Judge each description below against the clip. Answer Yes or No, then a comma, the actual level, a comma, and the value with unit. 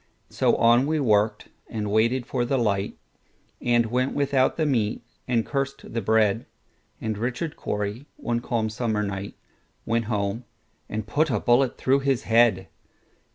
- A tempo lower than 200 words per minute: Yes, average, 140 wpm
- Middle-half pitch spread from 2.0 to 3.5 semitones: Yes, average, 3.2 semitones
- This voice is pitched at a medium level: No, low, 115 Hz